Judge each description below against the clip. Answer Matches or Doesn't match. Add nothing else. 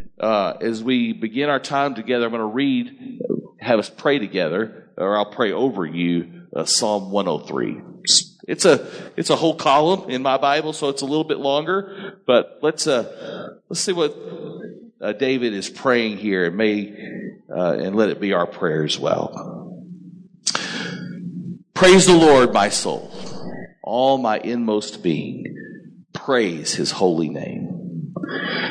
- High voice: Doesn't match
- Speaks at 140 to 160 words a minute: Matches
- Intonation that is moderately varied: Doesn't match